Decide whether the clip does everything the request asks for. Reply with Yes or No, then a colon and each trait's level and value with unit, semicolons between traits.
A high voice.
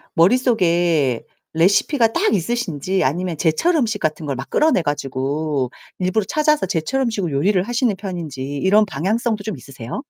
No: medium, 180 Hz